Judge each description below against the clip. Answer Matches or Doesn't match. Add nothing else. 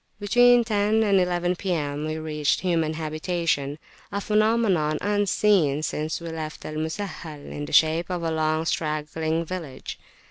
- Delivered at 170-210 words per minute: Doesn't match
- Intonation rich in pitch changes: Doesn't match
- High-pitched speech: Doesn't match